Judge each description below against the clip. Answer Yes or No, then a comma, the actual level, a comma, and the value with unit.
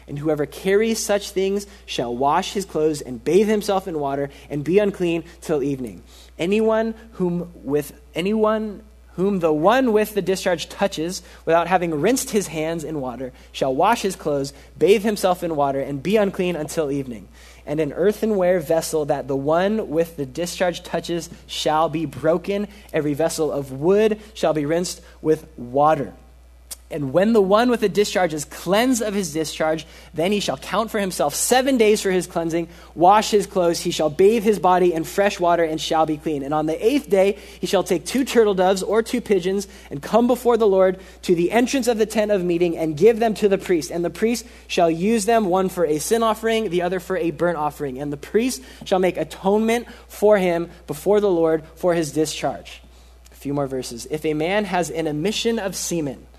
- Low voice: No, medium, 175 Hz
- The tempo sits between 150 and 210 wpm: Yes, average, 200 wpm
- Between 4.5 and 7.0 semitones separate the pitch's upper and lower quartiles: Yes, average, 4.9 semitones